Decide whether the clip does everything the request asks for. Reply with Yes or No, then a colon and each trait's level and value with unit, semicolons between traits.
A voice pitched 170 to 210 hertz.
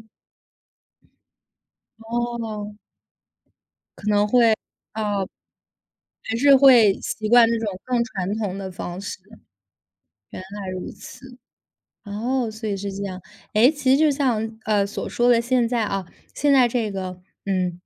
No: high, 220 Hz